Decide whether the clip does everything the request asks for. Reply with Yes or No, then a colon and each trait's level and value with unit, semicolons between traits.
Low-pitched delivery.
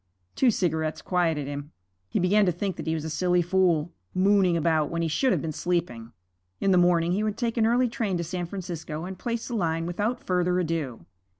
No: medium, 175 Hz